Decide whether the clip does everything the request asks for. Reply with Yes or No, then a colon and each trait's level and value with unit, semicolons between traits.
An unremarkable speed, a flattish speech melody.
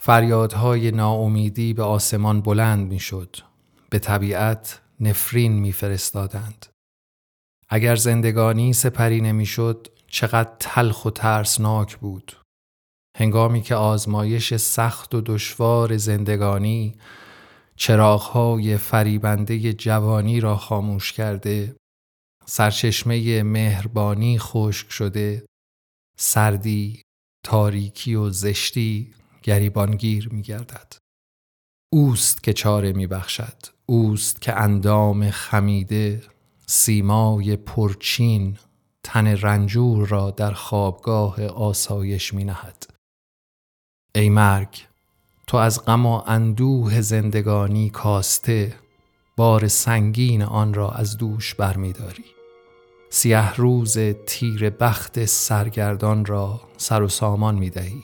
No: slow, 95 wpm; narrow, 1.9 semitones